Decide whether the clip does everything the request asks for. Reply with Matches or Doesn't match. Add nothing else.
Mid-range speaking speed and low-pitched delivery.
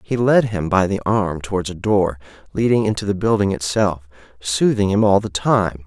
Matches